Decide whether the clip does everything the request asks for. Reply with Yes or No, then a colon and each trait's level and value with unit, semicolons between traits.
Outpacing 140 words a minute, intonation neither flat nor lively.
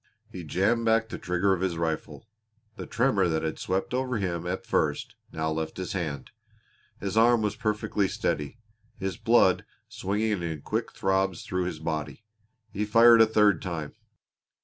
Yes: average, 165 wpm; average, 4.5 semitones